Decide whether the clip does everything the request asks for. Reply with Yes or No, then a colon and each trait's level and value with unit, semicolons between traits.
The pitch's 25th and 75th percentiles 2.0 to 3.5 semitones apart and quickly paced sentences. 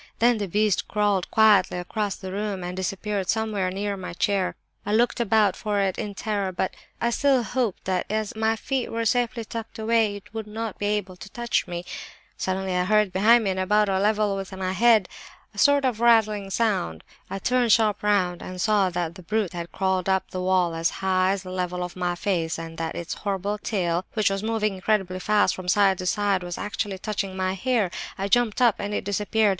Yes: average, 2.7 semitones; fast, 215 wpm